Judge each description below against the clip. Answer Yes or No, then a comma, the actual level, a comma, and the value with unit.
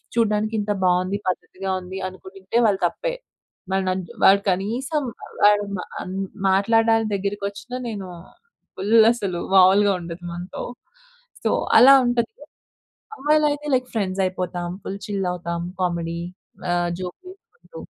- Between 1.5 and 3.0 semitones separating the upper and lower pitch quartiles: No, average, 3.5 semitones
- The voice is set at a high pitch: Yes, high, 195 Hz